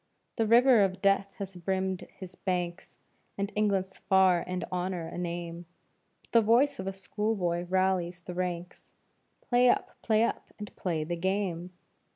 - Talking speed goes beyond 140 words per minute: Yes, average, 160 wpm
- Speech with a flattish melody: Yes, narrow, 2.3 semitones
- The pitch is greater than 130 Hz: Yes, high, 190 Hz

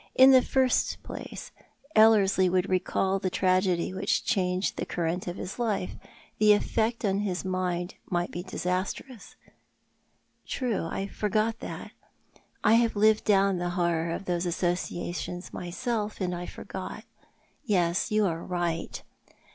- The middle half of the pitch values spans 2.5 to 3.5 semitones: Yes, average, 3.2 semitones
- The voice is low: No, medium, 185 Hz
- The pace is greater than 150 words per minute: No, average, 145 wpm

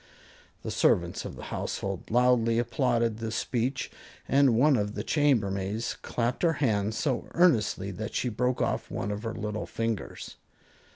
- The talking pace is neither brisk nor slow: Yes, average, 155 wpm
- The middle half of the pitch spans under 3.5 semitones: Yes, average, 3.0 semitones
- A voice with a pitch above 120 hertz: No, low, 115 Hz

